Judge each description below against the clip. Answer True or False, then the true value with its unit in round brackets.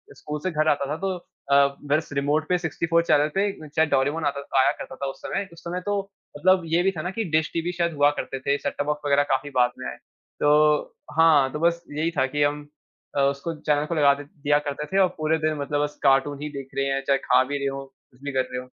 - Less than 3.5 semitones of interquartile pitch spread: True (2.6 semitones)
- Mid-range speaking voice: True (145 Hz)